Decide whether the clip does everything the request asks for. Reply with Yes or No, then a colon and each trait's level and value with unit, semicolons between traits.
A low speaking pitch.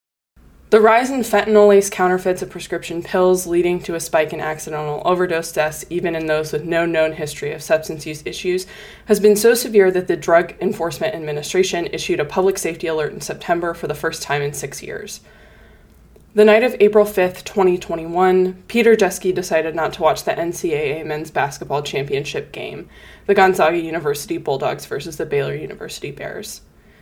No: medium, 180 Hz